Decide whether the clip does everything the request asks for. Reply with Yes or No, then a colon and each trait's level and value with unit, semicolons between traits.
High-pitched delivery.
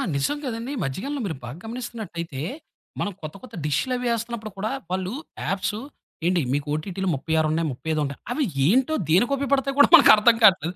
Yes: high, 195 Hz